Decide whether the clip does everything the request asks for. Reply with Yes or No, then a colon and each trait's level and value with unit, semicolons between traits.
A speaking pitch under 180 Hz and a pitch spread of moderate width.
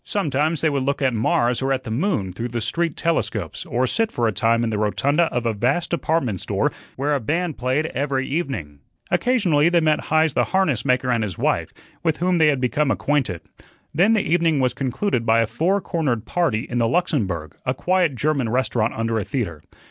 No: low, 135 Hz; wide, 5.9 semitones